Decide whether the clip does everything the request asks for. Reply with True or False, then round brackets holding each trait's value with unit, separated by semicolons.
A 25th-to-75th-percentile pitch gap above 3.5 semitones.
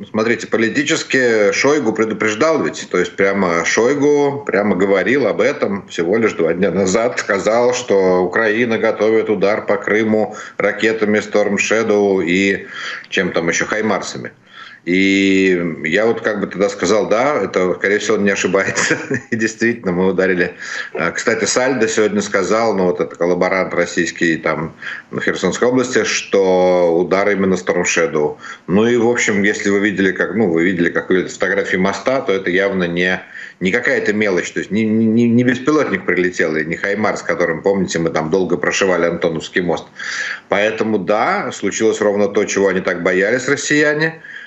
False (3.1 semitones)